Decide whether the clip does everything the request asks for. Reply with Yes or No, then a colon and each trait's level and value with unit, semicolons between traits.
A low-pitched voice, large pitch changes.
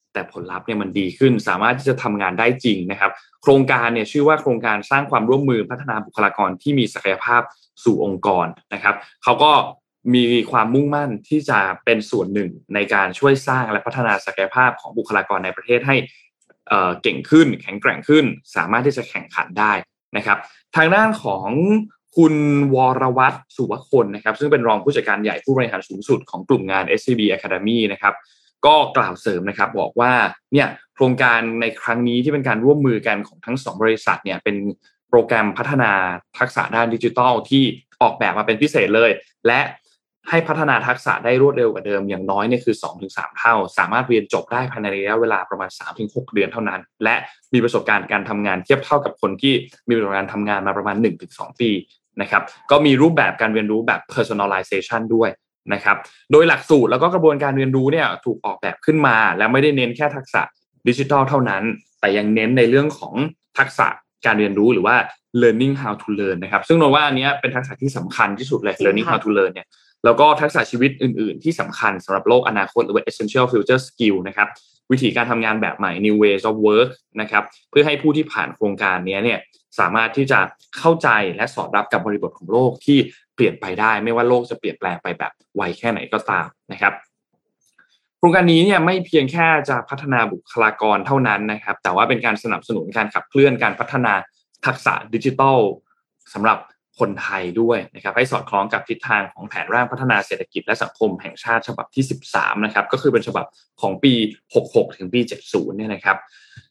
No: low, 120 Hz; average, 4.8 semitones